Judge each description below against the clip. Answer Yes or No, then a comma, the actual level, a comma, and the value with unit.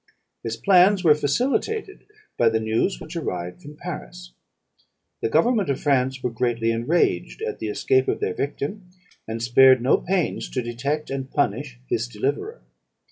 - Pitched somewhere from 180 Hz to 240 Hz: No, low, 130 Hz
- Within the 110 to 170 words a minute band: Yes, average, 155 wpm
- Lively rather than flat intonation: Yes, wide, 5.7 semitones